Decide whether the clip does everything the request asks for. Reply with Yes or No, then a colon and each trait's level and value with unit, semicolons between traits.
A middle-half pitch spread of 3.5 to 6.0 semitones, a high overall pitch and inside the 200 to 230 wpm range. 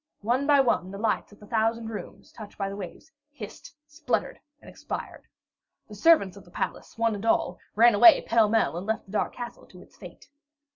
No: average, 2.7 semitones; high, 220 Hz; fast, 205 wpm